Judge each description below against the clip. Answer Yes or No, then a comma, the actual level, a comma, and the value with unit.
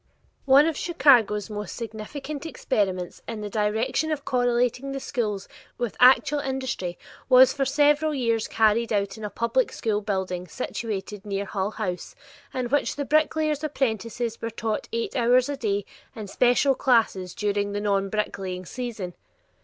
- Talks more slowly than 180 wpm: Yes, average, 155 wpm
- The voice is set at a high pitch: Yes, high, 230 Hz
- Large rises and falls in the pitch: No, average, 4.4 semitones